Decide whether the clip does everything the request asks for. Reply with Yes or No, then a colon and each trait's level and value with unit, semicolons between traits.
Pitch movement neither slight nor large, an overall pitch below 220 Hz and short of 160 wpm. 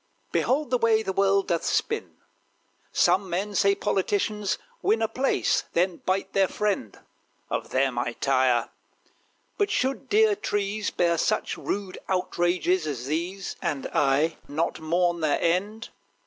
Yes: average, 4.4 semitones; medium, 185 Hz; average, 140 wpm